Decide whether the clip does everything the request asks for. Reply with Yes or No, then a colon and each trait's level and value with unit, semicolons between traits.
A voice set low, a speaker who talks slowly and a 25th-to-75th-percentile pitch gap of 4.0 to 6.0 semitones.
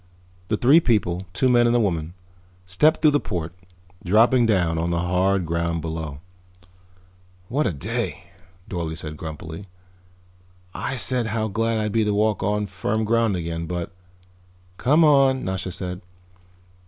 No: very low, 95 Hz; average, 155 wpm; average, 5.0 semitones